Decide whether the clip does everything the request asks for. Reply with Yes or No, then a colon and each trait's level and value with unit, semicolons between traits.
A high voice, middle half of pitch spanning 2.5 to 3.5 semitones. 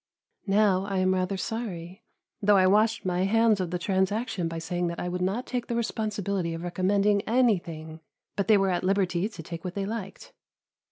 Yes: high, 195 Hz; average, 3.0 semitones